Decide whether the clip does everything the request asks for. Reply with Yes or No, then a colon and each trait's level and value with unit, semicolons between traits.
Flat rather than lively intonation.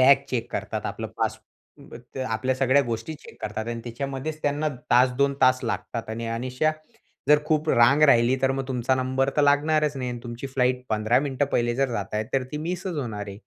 No: average, 3.2 semitones